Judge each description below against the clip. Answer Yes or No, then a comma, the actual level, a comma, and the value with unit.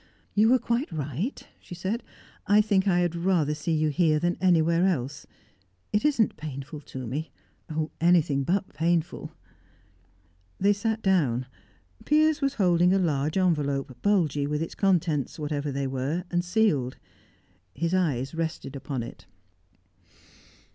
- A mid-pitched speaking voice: Yes, medium, 165 Hz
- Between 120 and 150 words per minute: Yes, average, 140 wpm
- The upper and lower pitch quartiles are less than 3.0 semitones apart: No, average, 4.7 semitones